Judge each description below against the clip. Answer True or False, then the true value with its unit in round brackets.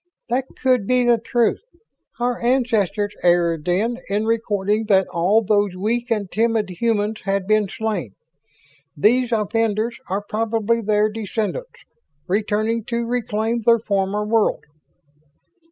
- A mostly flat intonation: True (2.3 semitones)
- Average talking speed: False (125 wpm)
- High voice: True (215 Hz)